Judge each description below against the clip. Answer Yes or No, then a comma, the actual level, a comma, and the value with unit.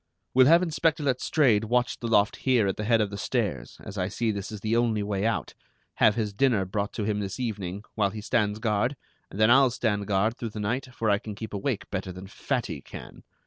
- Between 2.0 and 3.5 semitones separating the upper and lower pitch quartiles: Yes, average, 2.9 semitones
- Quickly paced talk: Yes, fast, 230 wpm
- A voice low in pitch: Yes, low, 110 Hz